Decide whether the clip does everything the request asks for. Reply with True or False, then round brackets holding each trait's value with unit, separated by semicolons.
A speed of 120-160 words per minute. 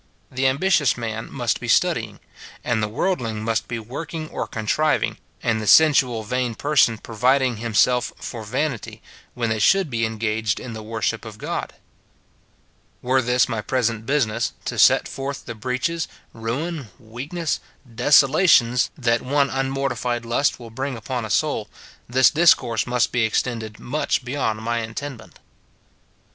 True (150 wpm)